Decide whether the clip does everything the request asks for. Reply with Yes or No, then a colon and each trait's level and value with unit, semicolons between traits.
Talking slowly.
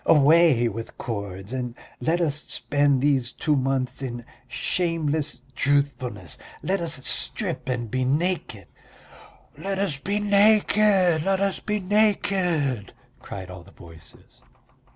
Yes: slow, 125 wpm